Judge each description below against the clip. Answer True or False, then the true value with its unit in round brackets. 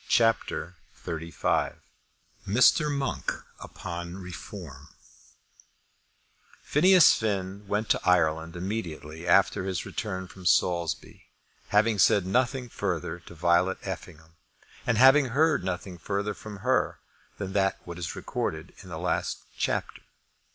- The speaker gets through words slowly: True (115 wpm)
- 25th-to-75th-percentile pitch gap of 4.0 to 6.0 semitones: True (4.4 semitones)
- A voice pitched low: True (95 Hz)